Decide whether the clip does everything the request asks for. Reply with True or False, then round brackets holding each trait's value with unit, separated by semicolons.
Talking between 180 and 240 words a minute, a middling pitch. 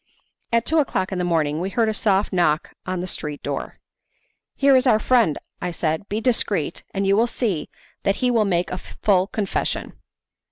False (195 wpm; 195 Hz)